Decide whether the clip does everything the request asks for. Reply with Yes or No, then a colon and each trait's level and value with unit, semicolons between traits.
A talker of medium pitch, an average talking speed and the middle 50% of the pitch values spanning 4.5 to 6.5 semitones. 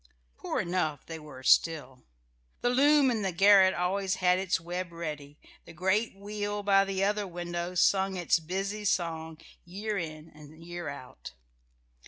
No: medium, 180 Hz; average, 155 wpm; average, 3.5 semitones